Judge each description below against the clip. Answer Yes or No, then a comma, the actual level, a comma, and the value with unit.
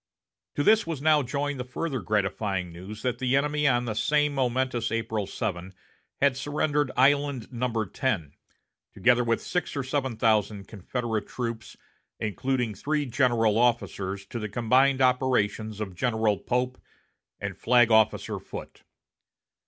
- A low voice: Yes, low, 120 Hz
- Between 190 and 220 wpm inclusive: No, average, 140 wpm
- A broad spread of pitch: No, average, 3.8 semitones